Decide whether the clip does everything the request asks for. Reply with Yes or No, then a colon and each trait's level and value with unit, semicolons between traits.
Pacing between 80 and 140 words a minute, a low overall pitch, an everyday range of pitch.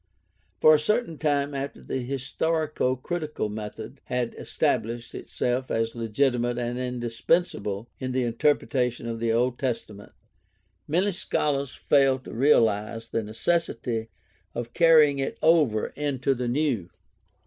Yes: slow, 135 wpm; low, 125 Hz; average, 3.9 semitones